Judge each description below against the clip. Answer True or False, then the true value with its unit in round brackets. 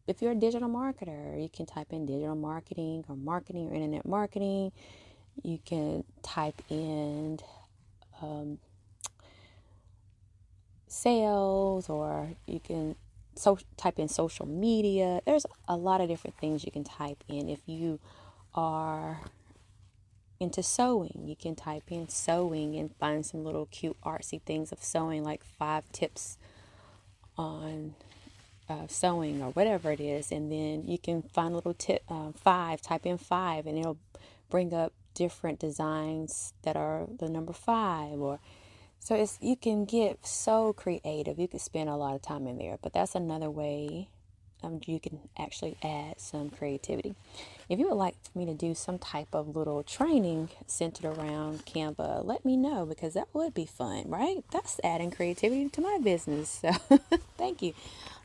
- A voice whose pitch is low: False (155 Hz)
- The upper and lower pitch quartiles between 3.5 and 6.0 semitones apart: True (3.9 semitones)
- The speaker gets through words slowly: False (160 wpm)